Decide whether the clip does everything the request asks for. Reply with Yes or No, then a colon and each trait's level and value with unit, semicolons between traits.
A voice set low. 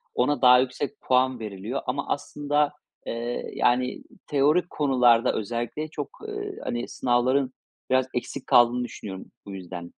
Yes: low, 125 Hz